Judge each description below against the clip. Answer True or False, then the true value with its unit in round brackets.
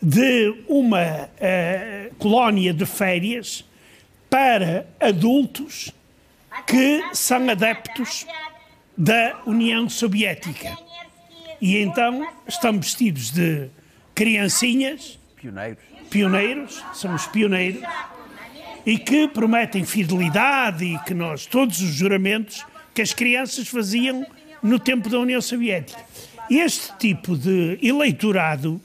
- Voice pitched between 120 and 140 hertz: False (225 Hz)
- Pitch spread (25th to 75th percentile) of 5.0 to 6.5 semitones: True (5.3 semitones)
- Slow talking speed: True (100 wpm)